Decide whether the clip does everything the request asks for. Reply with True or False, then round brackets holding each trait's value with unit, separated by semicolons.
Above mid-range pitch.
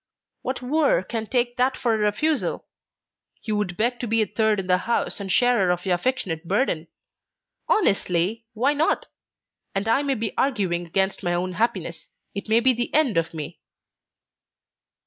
True (220 Hz)